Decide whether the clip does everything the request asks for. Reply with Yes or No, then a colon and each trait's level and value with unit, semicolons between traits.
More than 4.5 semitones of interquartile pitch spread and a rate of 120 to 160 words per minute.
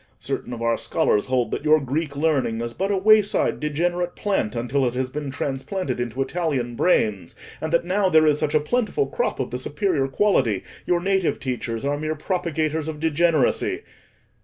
No: wide, 5.4 semitones; average, 185 wpm